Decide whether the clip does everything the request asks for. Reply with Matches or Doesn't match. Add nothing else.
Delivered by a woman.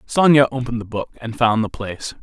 Doesn't match